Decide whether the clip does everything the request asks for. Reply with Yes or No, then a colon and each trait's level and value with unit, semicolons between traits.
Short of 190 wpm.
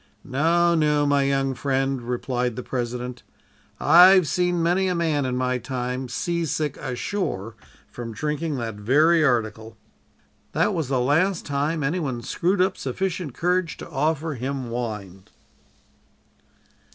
Yes: slow, 135 wpm